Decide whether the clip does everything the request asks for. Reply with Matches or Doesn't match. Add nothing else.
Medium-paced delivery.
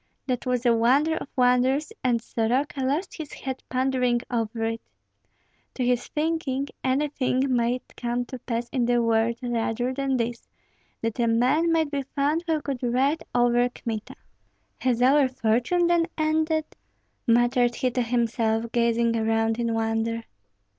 Matches